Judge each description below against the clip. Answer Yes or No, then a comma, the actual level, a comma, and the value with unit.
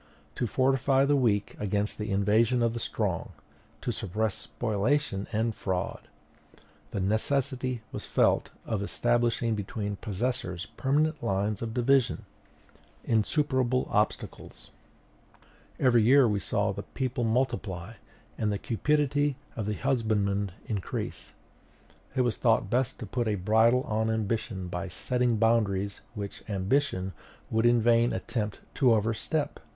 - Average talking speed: No, slow, 125 wpm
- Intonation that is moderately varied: Yes, average, 3.7 semitones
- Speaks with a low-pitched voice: Yes, low, 115 Hz